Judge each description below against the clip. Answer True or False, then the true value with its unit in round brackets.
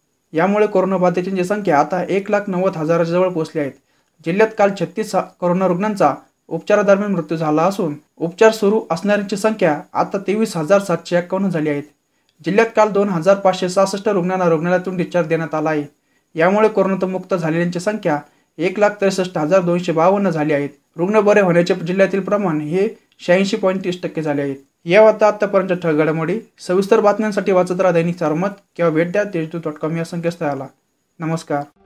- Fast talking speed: True (170 wpm)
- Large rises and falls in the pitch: False (3.5 semitones)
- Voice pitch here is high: False (180 Hz)